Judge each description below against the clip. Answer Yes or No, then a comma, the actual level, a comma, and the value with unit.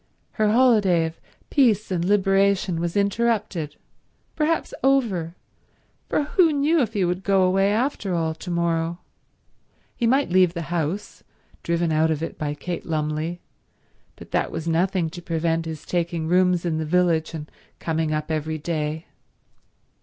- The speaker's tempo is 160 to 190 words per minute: No, average, 150 wpm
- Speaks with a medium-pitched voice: Yes, medium, 175 Hz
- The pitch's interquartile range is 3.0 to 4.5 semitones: Yes, average, 3.6 semitones